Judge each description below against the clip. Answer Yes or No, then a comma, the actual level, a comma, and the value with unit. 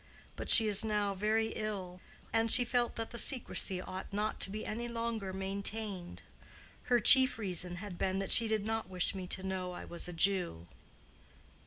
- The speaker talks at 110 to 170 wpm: No, average, 185 wpm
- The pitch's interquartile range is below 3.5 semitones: Yes, average, 3.0 semitones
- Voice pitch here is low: No, high, 200 Hz